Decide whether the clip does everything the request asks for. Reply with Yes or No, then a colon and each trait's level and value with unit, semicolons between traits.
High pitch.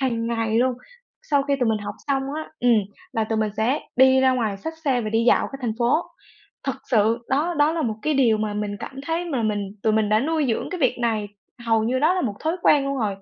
Yes: high, 240 Hz